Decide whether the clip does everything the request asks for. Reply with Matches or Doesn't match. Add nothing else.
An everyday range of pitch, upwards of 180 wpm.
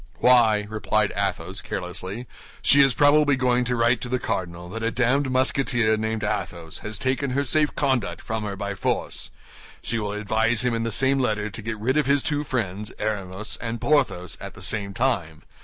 Matches